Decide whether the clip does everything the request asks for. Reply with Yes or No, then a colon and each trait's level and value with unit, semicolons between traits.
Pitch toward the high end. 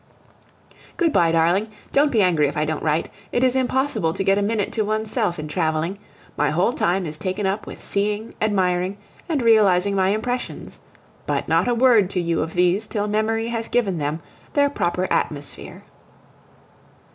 Yes: high, 200 Hz